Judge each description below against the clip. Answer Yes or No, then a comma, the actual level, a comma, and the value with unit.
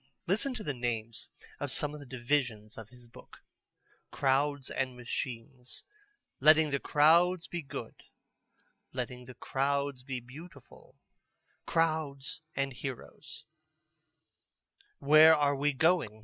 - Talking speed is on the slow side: Yes, slow, 120 wpm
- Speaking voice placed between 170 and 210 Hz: No, medium, 140 Hz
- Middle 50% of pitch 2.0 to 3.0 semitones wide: No, average, 3.5 semitones